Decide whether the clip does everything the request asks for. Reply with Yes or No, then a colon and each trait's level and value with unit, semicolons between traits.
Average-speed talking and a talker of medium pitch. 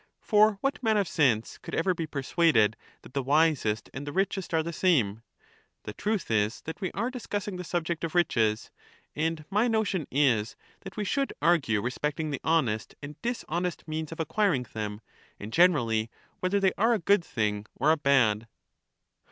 Yes: average, 175 wpm; medium, 160 Hz